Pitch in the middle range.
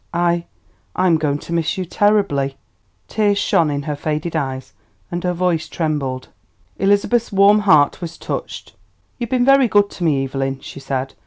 Yes: medium, 170 Hz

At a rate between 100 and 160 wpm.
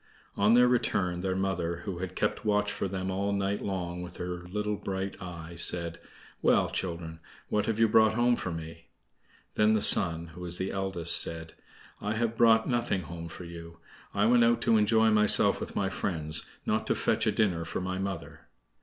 No: average, 195 wpm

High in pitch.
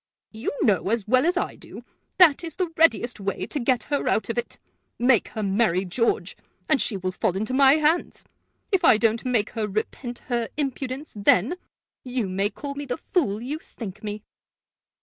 Yes: high, 240 Hz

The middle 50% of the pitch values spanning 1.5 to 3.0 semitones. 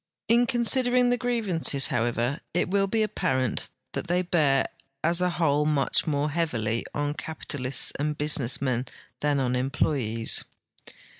No: wide, 5.4 semitones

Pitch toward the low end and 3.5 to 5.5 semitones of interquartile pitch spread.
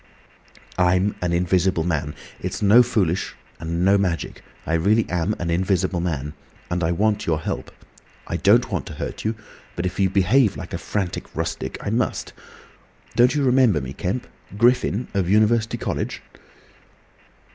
Yes: very low, 95 Hz; average, 3.9 semitones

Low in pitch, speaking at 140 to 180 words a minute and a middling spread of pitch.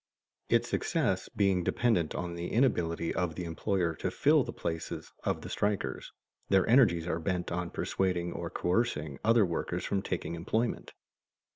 Yes: very low, 90 Hz; average, 155 wpm; average, 3.2 semitones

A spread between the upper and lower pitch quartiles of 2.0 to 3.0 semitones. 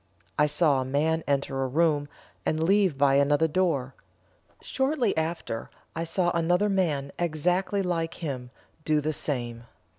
No: average, 3.9 semitones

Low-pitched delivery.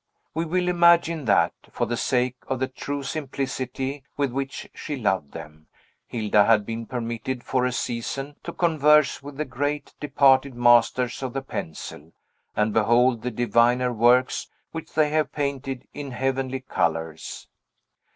Yes: low, 130 Hz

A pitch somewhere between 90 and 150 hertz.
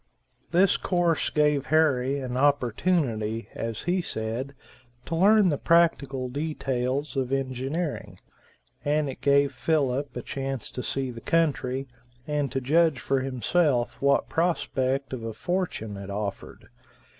Yes: low, 135 Hz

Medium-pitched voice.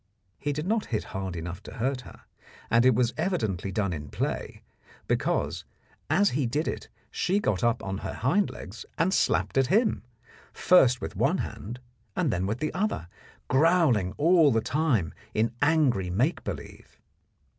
No: low, 125 Hz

